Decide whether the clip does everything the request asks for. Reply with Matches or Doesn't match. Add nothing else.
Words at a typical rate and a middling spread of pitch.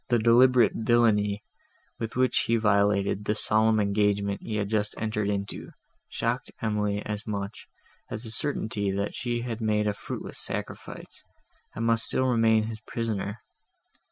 Doesn't match